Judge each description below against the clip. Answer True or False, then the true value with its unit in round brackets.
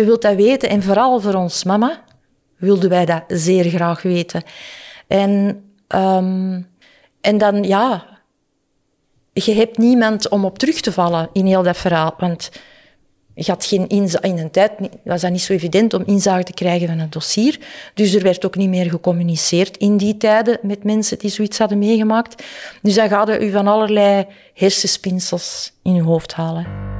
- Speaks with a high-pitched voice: True (195 Hz)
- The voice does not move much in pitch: False (3.0 semitones)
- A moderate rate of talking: True (175 wpm)